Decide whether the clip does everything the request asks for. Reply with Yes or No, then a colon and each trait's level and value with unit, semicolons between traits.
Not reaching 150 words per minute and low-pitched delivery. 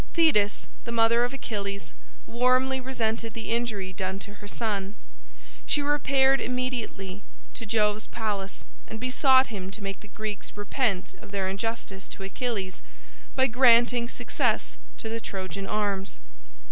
No: average, 140 wpm; high, 220 Hz